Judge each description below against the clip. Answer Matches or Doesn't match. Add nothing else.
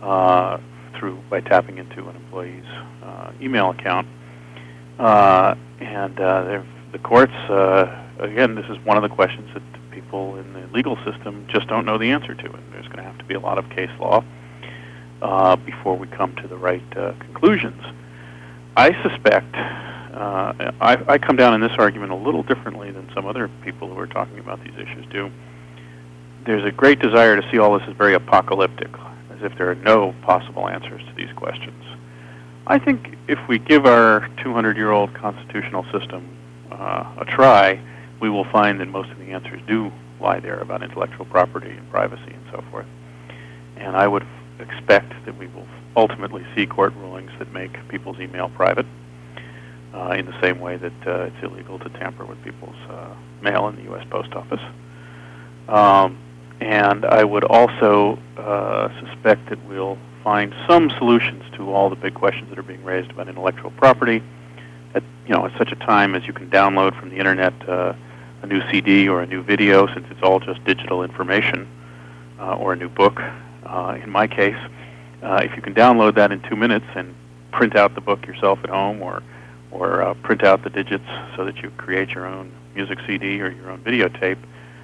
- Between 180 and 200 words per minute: Matches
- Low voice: Matches